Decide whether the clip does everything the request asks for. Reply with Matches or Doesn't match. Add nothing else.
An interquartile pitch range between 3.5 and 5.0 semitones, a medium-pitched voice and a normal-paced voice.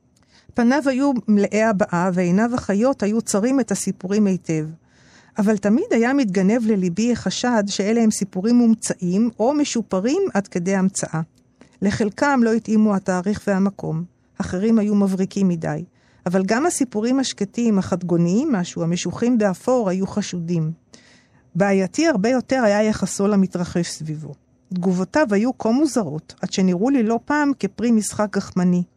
Doesn't match